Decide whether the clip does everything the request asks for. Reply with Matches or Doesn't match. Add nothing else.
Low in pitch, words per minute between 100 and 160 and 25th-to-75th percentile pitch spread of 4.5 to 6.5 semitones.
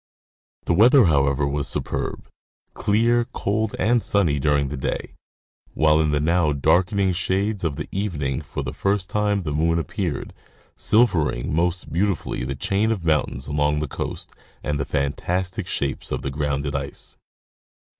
Matches